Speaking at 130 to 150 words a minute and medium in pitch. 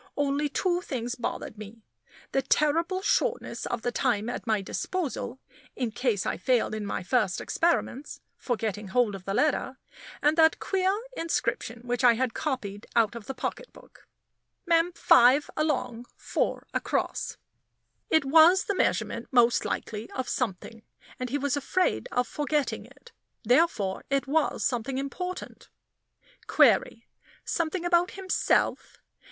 No: average, 140 wpm; very high, 265 Hz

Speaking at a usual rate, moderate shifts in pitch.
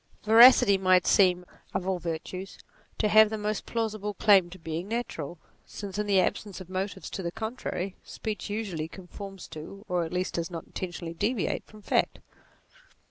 Yes: average, 180 wpm; average, 3.0 semitones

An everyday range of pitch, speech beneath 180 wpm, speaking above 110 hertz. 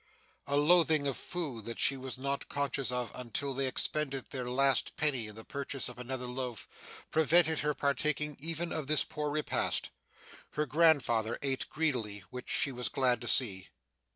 Yes: average, 3.3 semitones; average, 170 wpm; low, 135 Hz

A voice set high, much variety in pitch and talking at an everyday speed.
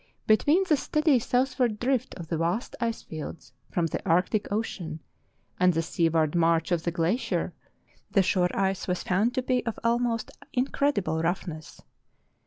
Yes: high, 195 Hz; wide, 6.6 semitones; average, 155 wpm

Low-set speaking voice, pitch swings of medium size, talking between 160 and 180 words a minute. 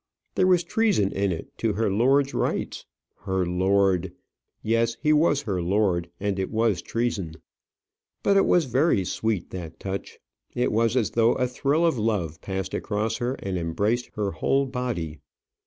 Yes: low, 110 Hz; average, 4.9 semitones; average, 165 wpm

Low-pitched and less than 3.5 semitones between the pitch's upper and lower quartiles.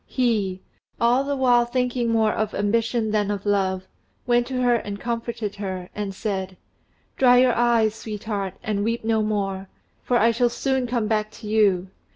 No: high, 220 Hz; average, 2.9 semitones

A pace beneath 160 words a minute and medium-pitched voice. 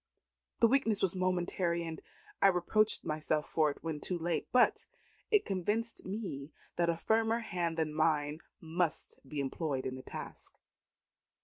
Yes: average, 150 wpm; medium, 170 Hz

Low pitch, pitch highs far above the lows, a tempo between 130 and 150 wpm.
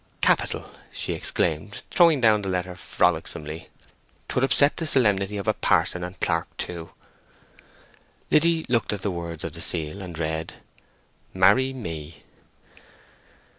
Yes: very low, 95 Hz; wide, 6.8 semitones; slow, 135 wpm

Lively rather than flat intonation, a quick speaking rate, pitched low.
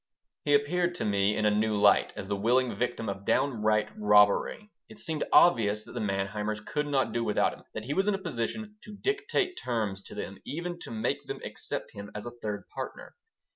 Yes: wide, 7.8 semitones; fast, 210 wpm; low, 115 Hz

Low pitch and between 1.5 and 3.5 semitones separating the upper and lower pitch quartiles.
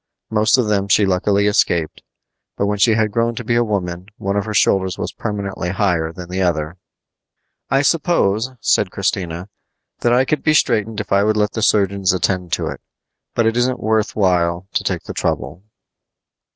Yes: low, 100 Hz; average, 3.1 semitones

